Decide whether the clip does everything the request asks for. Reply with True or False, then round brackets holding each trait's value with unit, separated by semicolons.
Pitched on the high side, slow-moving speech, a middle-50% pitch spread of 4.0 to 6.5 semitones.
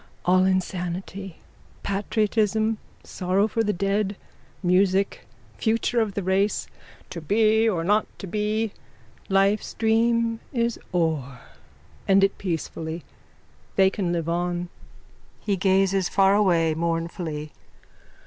False (195 Hz; 115 wpm; 3.2 semitones)